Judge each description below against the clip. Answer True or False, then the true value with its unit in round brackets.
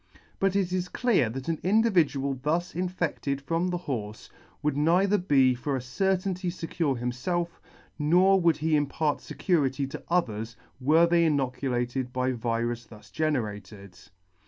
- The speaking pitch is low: False (150 Hz)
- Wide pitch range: True (5.7 semitones)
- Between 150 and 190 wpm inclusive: False (140 wpm)